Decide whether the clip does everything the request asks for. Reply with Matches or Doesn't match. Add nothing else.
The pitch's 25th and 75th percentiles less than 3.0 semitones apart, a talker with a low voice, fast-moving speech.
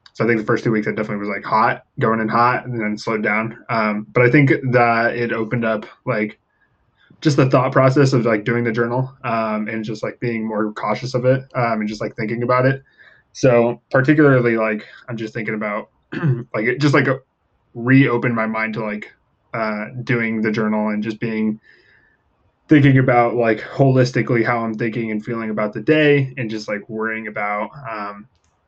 Doesn't match